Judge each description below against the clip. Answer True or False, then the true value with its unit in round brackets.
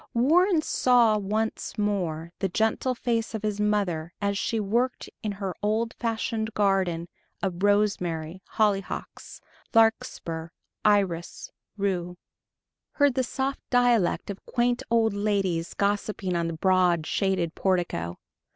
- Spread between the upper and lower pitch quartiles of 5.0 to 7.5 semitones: False (3.9 semitones)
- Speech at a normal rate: False (125 wpm)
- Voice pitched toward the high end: True (205 Hz)